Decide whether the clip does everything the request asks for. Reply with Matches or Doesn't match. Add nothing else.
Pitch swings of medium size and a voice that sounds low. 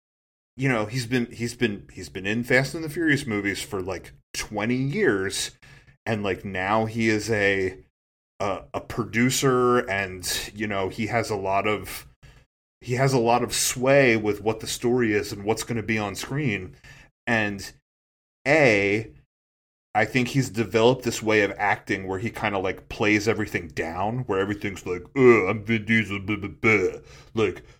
Matches